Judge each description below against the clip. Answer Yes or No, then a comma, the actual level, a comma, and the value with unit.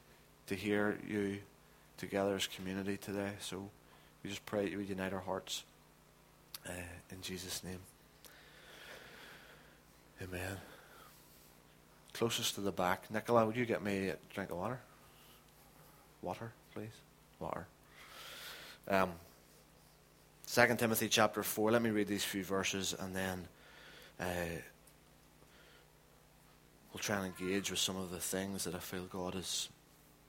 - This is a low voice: Yes, very low, 95 Hz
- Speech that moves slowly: Yes, slow, 130 wpm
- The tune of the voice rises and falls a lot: No, narrow, 2.4 semitones